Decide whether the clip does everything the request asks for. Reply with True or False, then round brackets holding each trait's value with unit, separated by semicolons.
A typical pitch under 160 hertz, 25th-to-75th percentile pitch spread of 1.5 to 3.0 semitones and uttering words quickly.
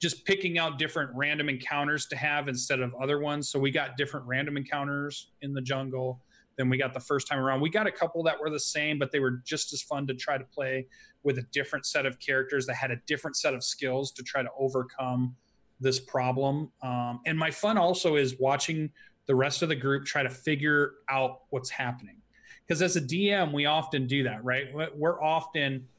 True (140 Hz; 2.6 semitones; 215 wpm)